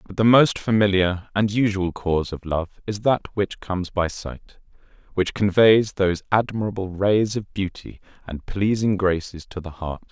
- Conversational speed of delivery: Yes, average, 165 wpm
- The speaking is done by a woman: No, male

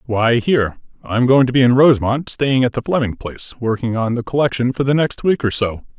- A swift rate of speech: Yes, fast, 230 wpm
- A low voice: Yes, low, 125 Hz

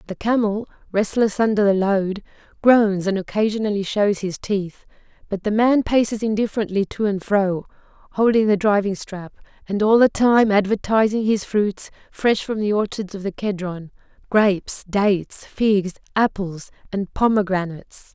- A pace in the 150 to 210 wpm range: No, average, 140 wpm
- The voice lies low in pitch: No, high, 205 Hz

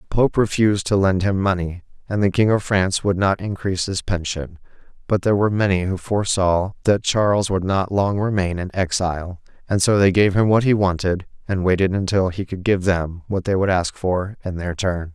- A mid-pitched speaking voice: No, very low, 95 Hz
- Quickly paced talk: Yes, fast, 215 wpm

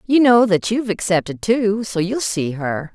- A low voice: No, high, 205 Hz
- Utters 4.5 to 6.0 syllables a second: Yes, 4.6 syllables/s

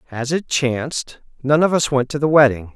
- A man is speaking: Yes, male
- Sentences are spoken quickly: Yes, fast, 220 wpm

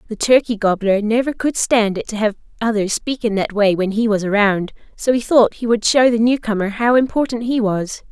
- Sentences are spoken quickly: Yes, fast, 220 wpm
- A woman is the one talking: Yes, female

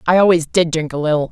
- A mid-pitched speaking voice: Yes, medium, 165 Hz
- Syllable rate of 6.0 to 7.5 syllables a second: Yes, 6.8 syllables/s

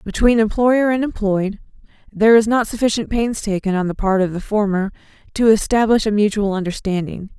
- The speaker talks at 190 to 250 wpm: No, average, 170 wpm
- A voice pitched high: Yes, high, 210 Hz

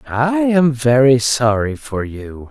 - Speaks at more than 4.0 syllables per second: No, 3.4 syllables/s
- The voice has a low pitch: Yes, low, 120 Hz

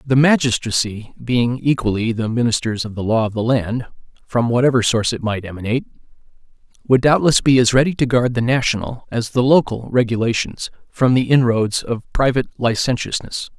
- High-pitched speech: No, low, 120 Hz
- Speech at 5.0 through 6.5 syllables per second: Yes, 5.5 syllables/s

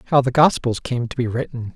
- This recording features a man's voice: Yes, male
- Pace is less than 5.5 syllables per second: No, 6.0 syllables/s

